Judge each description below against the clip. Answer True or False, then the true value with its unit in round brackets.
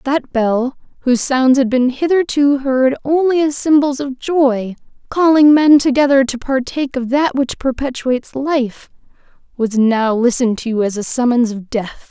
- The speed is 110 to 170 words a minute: True (150 wpm)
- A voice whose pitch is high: True (260 Hz)